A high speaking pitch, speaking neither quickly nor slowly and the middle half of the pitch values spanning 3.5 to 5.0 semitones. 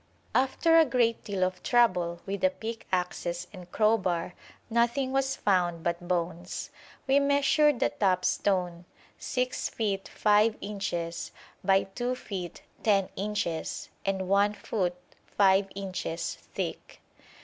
No: high, 195 Hz; slow, 125 wpm; average, 4.7 semitones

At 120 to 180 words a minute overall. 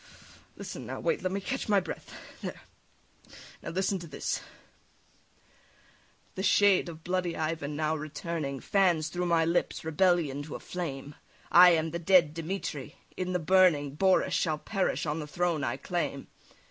Yes: average, 160 wpm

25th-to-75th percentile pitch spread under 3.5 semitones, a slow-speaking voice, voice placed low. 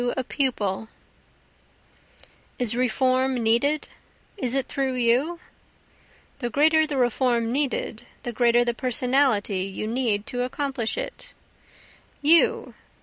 No: average, 2.8 semitones; slow, 115 wpm; very high, 250 Hz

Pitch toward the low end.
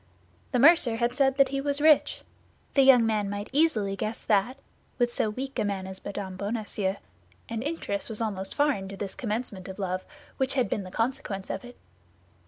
No: high, 225 Hz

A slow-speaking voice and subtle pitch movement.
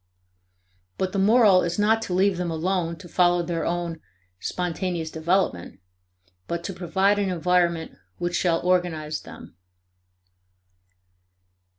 Yes: slow, 120 wpm; narrow, 2.1 semitones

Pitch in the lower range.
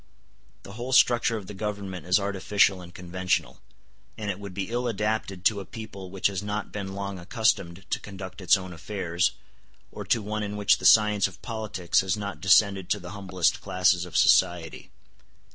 Yes: low, 100 Hz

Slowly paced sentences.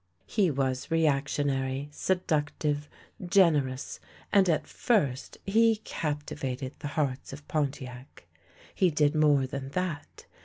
Yes: slow, 110 wpm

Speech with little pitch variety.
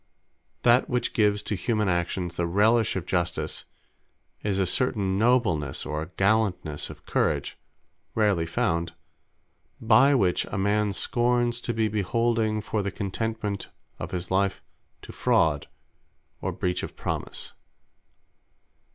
No: average, 4.0 semitones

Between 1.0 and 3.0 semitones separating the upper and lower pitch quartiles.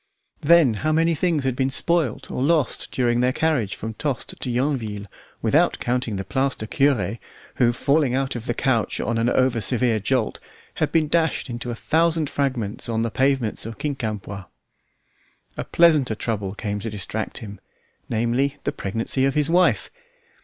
No: average, 4.2 semitones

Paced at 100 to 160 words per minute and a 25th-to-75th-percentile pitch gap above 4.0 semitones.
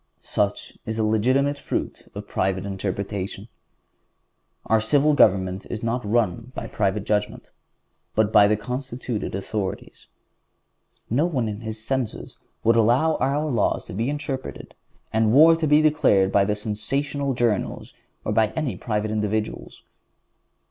Yes: slow, 135 wpm; average, 4.4 semitones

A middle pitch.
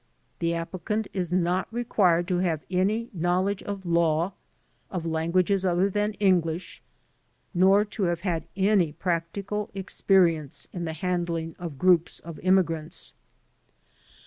Yes: medium, 180 Hz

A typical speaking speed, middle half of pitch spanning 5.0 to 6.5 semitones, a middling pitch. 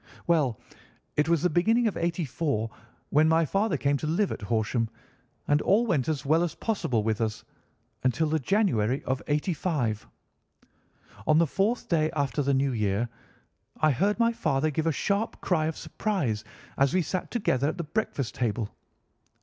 Yes: average, 170 wpm; wide, 5.6 semitones; medium, 155 Hz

